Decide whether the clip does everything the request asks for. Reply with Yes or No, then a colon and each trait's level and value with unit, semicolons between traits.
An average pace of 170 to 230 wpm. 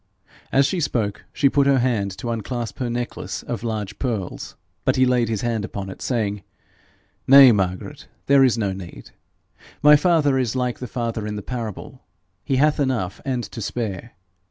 Yes: average, 180 wpm